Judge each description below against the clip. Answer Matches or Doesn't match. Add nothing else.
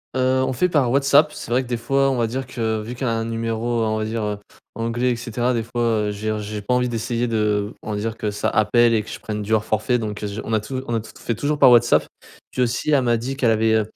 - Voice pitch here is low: Matches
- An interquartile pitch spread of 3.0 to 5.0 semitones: Doesn't match